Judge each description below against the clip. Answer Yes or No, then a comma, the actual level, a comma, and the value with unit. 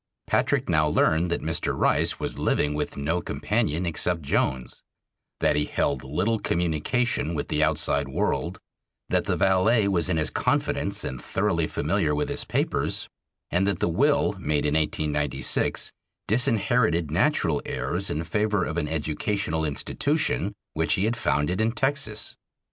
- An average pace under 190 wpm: Yes, average, 150 wpm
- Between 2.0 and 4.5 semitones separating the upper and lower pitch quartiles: No, average, 5.2 semitones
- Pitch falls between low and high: No, very low, 85 Hz